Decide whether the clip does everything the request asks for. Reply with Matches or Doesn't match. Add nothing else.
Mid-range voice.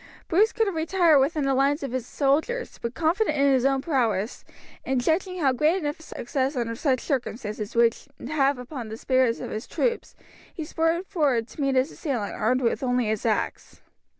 Doesn't match